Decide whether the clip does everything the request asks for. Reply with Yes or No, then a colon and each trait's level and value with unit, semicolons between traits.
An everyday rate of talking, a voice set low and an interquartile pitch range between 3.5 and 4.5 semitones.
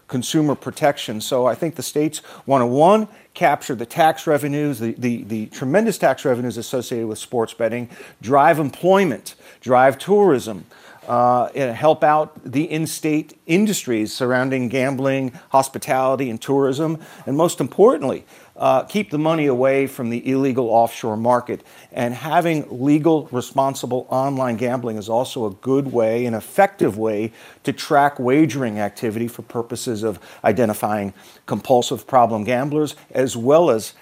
Yes: average, 145 wpm; low, 130 Hz; average, 4.2 semitones